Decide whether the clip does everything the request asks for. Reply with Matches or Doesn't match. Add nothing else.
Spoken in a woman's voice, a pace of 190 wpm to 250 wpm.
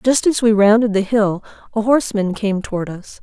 Matches